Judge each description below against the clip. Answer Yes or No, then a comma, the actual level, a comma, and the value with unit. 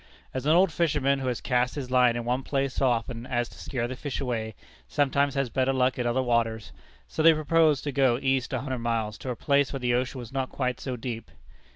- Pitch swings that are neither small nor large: No, narrow, 2.2 semitones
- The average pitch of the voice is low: Yes, low, 130 Hz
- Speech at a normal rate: No, fast, 240 wpm